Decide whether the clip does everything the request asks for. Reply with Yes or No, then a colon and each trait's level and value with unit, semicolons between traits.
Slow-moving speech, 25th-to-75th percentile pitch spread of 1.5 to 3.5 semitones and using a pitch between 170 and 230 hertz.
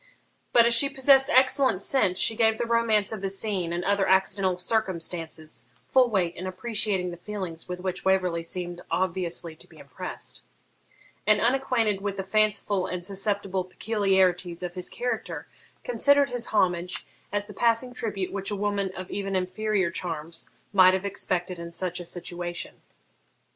No: average, 160 wpm; average, 3.2 semitones; high, 190 Hz